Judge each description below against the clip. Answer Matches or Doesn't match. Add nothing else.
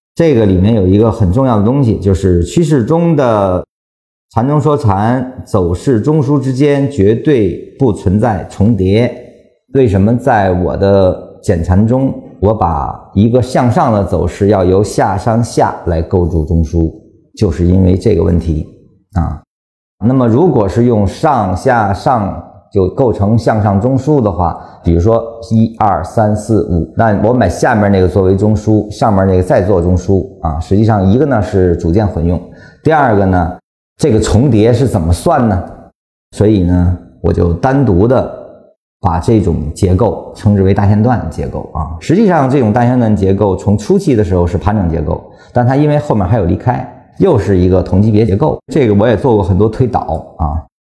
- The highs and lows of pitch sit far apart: Doesn't match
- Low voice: Matches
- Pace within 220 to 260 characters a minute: Matches